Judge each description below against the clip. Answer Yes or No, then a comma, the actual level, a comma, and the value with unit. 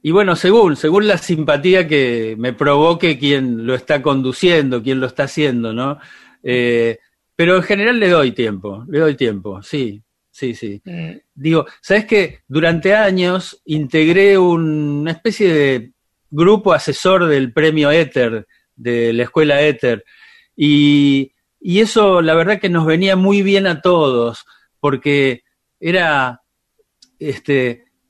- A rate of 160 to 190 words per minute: No, average, 135 wpm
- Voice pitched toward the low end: No, medium, 150 Hz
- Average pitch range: No, wide, 6.0 semitones